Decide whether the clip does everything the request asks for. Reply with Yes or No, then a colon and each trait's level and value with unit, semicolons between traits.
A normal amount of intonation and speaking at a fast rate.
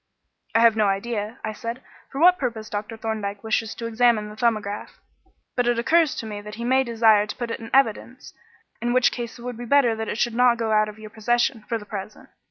No: narrow, 2.1 semitones; fast, 235 wpm